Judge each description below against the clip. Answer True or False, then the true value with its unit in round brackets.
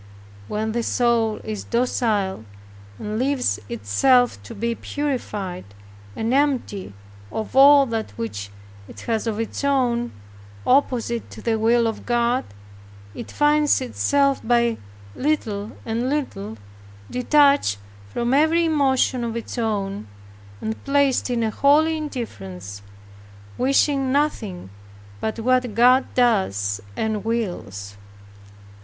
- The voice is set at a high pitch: True (235 Hz)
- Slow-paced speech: True (115 wpm)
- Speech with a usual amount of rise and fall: True (4.4 semitones)